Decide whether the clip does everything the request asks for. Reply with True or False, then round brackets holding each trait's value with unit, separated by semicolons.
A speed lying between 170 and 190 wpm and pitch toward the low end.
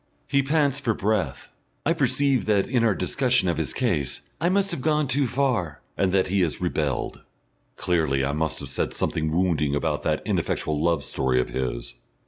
True (185 wpm; 95 Hz)